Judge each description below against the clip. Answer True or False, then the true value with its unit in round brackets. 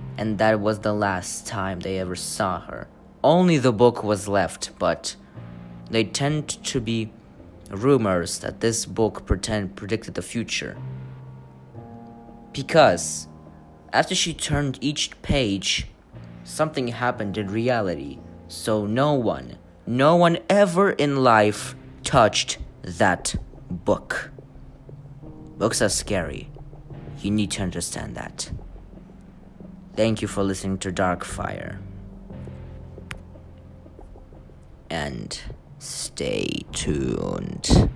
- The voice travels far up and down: True (6.4 semitones)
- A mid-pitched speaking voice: False (105 Hz)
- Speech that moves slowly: True (105 wpm)